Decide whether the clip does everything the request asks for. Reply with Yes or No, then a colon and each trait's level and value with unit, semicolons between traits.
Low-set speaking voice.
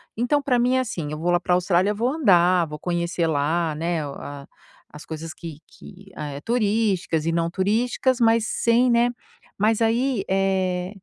No: medium, 185 Hz